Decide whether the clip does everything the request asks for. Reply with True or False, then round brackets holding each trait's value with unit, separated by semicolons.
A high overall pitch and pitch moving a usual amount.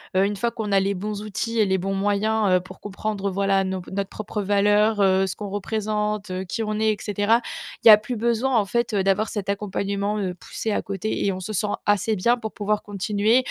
False (205 Hz; 1.8 semitones)